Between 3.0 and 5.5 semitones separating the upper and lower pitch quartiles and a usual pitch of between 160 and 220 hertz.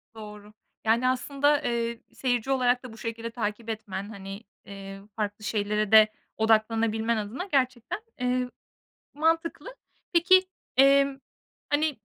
No: average, 4.0 semitones; high, 230 Hz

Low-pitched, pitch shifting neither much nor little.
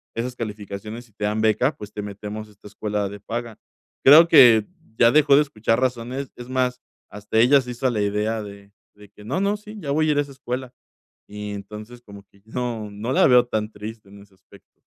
Yes: low, 110 Hz; average, 3.4 semitones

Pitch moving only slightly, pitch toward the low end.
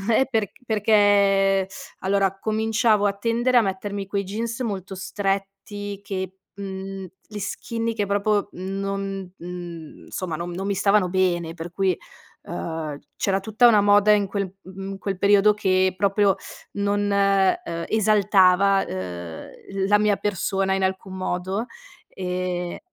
No: narrow, 1.5 semitones; high, 195 Hz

